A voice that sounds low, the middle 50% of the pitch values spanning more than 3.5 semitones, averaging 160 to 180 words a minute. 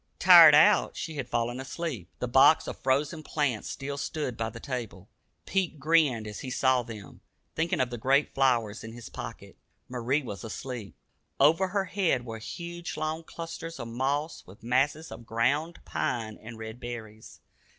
Yes: low, 130 Hz; average, 5.0 semitones; average, 170 wpm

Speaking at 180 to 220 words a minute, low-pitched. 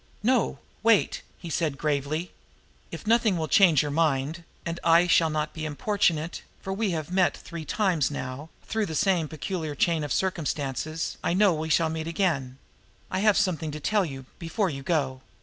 No: average, 185 wpm; medium, 165 Hz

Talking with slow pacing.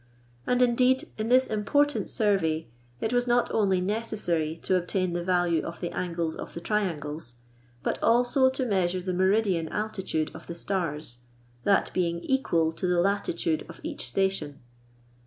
No: average, 155 wpm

